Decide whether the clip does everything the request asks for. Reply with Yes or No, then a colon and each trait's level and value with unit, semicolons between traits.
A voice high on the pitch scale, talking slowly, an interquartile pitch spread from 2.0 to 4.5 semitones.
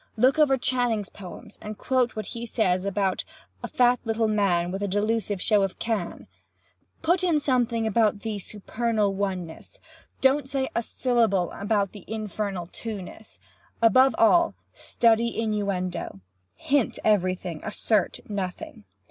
Yes: high, 215 Hz; slow, 130 wpm; average, 3.2 semitones